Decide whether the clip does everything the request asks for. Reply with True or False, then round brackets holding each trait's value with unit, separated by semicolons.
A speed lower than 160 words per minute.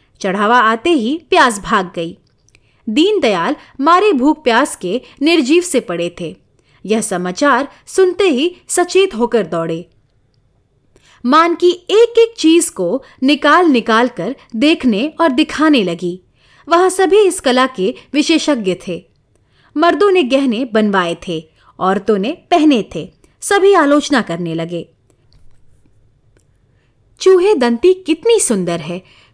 True (125 wpm)